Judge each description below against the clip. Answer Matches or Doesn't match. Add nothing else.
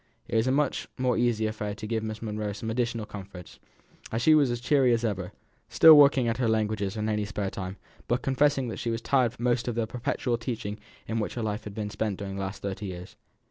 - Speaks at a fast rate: Matches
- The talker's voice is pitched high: Doesn't match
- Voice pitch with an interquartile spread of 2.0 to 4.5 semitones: Matches